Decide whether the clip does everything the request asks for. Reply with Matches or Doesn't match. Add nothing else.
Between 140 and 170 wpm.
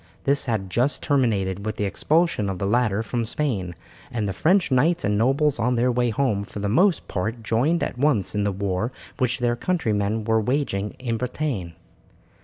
Doesn't match